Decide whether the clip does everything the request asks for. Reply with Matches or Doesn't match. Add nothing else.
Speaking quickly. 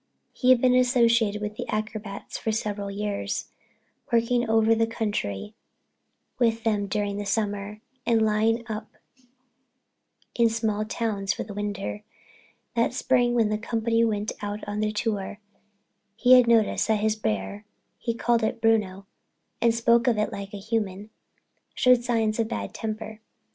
Doesn't match